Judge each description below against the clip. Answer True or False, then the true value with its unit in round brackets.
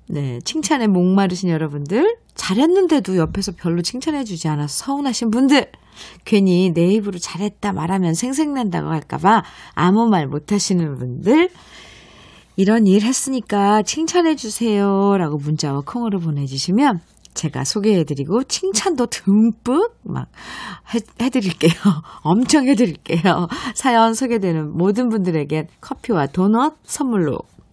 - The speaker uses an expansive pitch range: True (6.8 semitones)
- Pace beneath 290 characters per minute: False (295 characters per minute)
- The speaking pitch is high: True (200 Hz)